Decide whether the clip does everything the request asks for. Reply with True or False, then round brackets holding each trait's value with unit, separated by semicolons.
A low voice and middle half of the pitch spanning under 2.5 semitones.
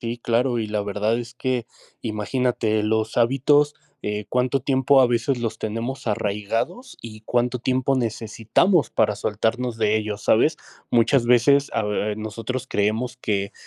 False (115 Hz; 2.9 semitones)